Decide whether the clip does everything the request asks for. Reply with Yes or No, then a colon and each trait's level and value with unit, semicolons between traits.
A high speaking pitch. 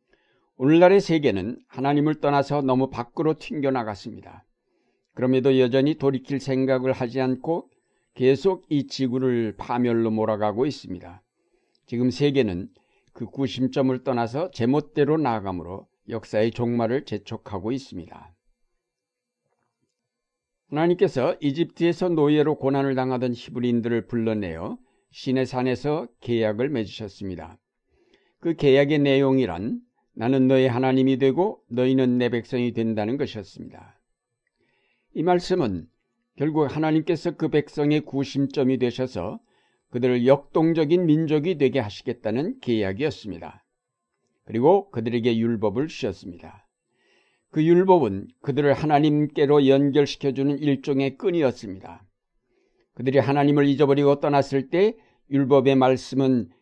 No: low, 135 Hz